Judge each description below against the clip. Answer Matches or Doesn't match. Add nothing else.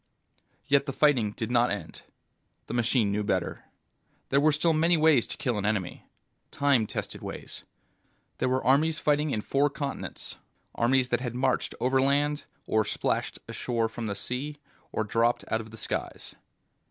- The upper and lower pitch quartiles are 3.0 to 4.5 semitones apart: Matches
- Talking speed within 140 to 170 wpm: Matches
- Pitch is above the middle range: Doesn't match